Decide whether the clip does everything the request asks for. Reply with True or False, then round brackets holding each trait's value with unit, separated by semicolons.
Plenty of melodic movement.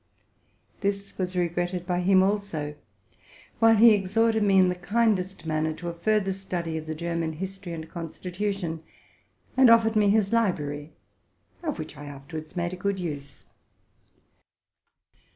False (3.7 semitones)